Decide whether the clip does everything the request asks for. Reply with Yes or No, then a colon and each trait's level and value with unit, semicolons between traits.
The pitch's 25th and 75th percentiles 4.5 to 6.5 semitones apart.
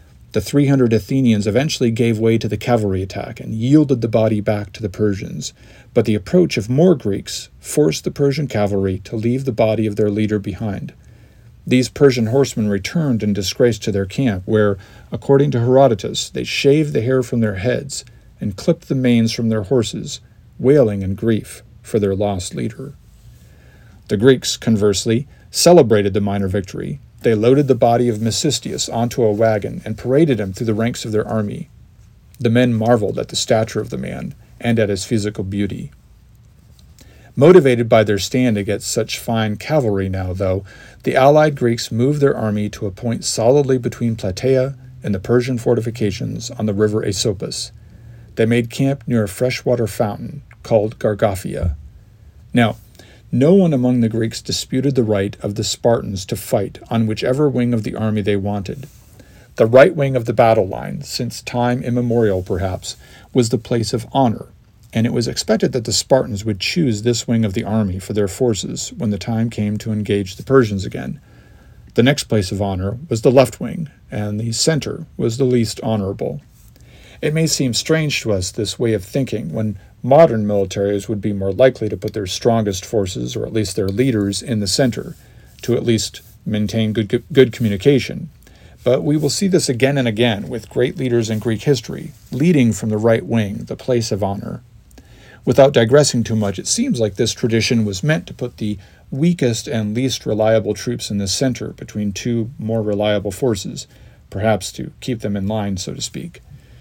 No: average, 3.2 semitones